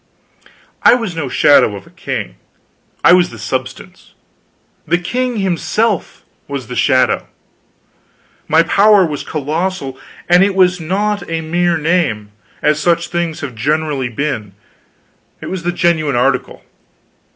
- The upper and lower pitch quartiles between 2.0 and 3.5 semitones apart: No, average, 4.4 semitones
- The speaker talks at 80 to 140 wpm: Yes, slow, 135 wpm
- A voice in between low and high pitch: Yes, medium, 165 Hz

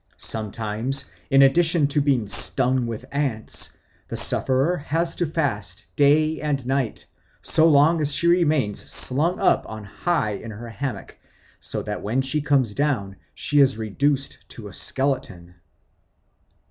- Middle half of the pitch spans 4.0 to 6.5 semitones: Yes, average, 5.0 semitones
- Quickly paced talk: No, average, 145 wpm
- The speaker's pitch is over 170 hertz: No, low, 135 Hz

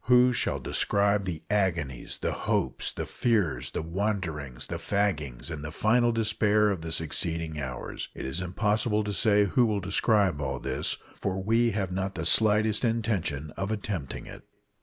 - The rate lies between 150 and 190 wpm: Yes, average, 165 wpm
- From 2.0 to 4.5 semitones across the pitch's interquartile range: No, average, 4.9 semitones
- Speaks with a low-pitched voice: Yes, low, 100 Hz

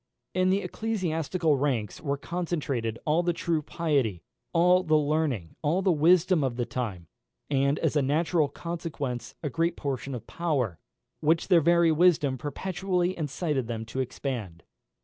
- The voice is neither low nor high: Yes, medium, 155 Hz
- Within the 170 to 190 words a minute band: No, average, 150 wpm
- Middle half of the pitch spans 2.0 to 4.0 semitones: No, average, 4.7 semitones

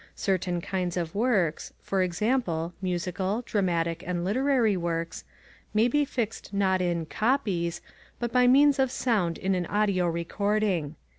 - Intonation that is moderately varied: Yes, average, 4.6 semitones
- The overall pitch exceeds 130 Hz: Yes, high, 190 Hz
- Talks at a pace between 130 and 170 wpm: Yes, average, 140 wpm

